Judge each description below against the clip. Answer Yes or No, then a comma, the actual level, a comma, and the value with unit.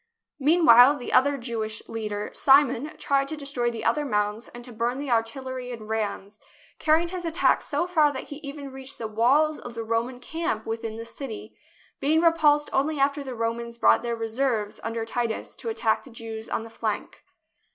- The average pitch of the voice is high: Yes, high, 245 Hz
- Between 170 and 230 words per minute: Yes, average, 190 wpm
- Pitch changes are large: No, average, 4.1 semitones